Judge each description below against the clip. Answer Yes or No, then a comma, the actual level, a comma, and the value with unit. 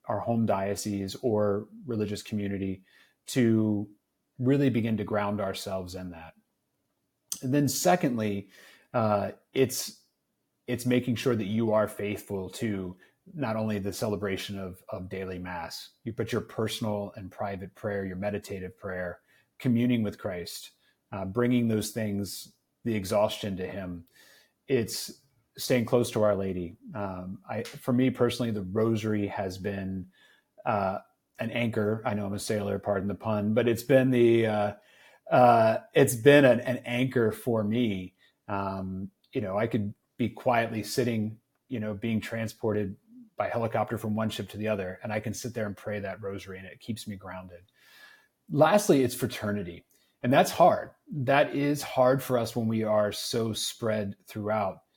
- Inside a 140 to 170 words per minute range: Yes, average, 160 wpm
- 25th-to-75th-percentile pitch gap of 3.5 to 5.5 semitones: No, average, 3.1 semitones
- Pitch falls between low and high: No, low, 110 Hz